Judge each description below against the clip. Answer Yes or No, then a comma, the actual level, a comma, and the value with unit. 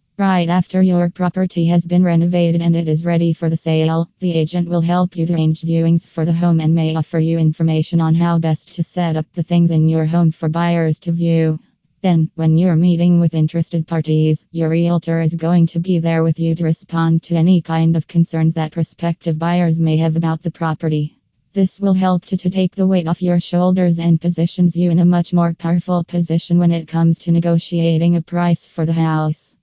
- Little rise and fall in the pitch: Yes, narrow, 1.2 semitones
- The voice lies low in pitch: No, medium, 170 Hz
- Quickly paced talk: Yes, fast, 215 wpm